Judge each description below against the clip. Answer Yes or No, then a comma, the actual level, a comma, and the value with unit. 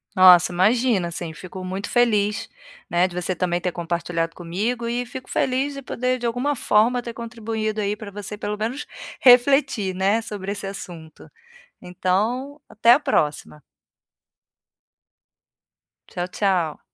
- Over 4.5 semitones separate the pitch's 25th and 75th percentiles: Yes, average, 5.0 semitones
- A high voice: Yes, high, 205 Hz